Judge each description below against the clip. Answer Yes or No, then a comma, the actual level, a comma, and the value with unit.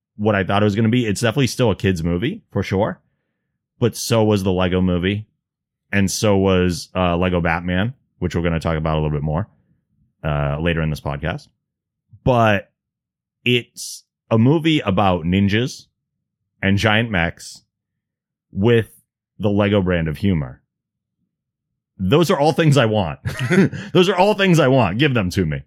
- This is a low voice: Yes, low, 100 Hz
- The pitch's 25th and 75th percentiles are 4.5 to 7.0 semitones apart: Yes, average, 5.3 semitones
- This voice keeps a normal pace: Yes, average, 175 wpm